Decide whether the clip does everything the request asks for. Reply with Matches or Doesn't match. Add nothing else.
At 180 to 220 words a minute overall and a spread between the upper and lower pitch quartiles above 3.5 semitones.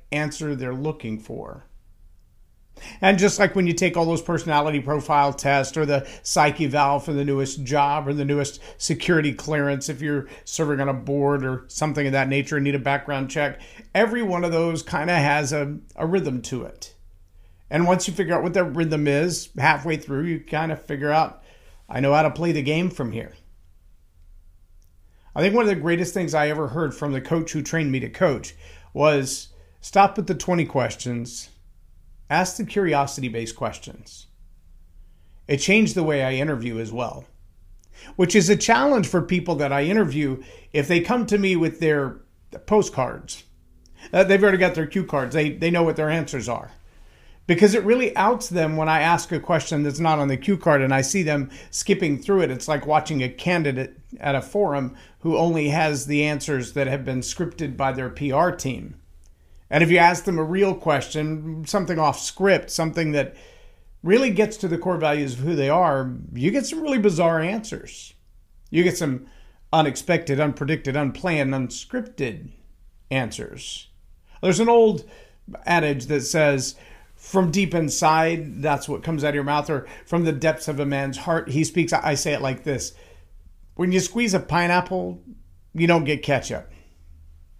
Matches